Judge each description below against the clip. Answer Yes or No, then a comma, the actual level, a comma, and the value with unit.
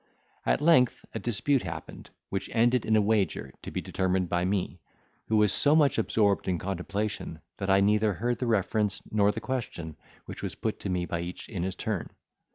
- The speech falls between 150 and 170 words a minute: No, average, 195 wpm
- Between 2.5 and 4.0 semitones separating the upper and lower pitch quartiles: Yes, average, 3.6 semitones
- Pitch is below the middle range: Yes, low, 100 Hz